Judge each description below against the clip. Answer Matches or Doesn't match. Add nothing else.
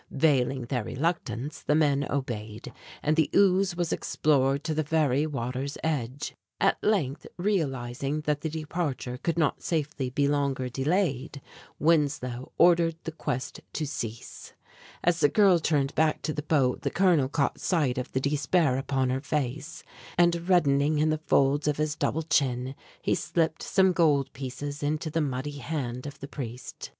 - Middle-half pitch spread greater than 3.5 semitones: Doesn't match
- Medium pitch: Matches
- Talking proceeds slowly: Doesn't match